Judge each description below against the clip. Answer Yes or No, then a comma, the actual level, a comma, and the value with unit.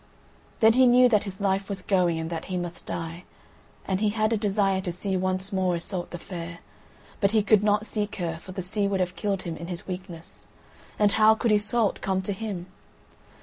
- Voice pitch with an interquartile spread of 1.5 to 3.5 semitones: Yes, average, 2.7 semitones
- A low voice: No, high, 195 Hz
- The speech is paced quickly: Yes, fast, 215 wpm